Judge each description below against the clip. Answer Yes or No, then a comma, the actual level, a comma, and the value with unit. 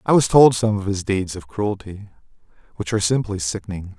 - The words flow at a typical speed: Yes, average, 195 wpm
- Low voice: Yes, low, 100 Hz